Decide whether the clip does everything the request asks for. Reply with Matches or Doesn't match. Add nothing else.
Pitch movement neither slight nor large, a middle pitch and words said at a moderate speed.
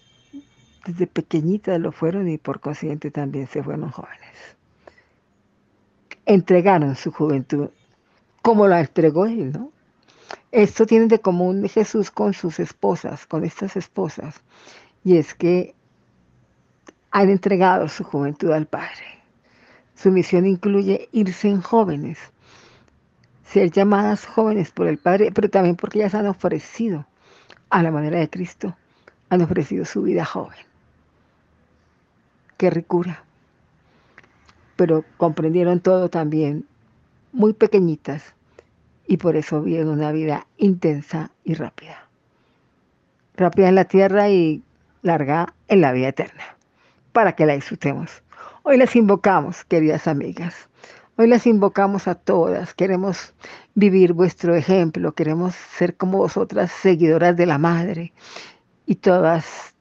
Doesn't match